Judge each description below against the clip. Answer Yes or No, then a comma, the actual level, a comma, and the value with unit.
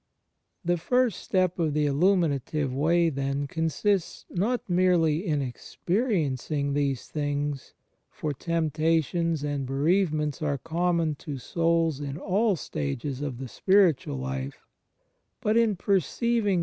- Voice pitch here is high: No, medium, 160 Hz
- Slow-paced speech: No, average, 145 wpm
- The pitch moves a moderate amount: Yes, average, 4.0 semitones